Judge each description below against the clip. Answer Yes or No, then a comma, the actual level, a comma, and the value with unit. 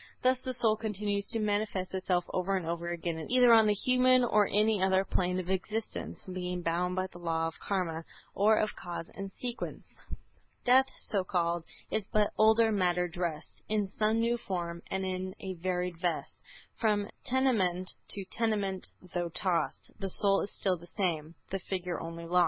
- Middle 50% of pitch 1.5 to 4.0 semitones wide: Yes, average, 3.3 semitones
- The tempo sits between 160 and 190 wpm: Yes, average, 175 wpm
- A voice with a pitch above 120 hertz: Yes, high, 190 Hz